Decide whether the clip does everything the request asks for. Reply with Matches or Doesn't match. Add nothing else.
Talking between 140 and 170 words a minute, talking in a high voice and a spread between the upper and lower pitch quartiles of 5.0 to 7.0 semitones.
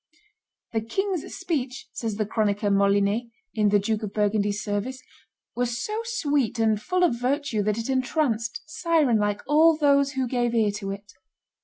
Matches